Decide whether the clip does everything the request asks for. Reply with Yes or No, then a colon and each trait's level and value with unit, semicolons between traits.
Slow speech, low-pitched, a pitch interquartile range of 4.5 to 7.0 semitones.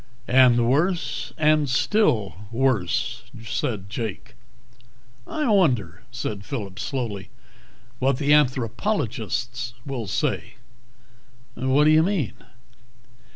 Yes: slow, 95 wpm; low, 125 Hz; average, 5.1 semitones